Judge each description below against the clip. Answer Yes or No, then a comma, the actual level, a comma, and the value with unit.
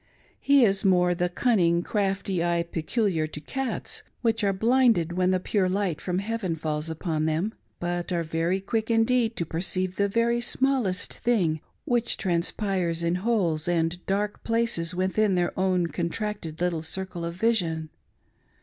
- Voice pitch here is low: No, medium, 185 Hz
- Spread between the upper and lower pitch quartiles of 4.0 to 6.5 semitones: Yes, average, 4.3 semitones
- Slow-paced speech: No, average, 155 wpm